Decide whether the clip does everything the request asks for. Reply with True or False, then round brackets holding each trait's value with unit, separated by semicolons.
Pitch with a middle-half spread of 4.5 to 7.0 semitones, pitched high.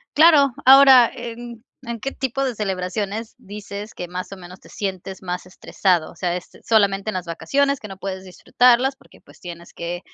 True (5.1 semitones; 205 Hz)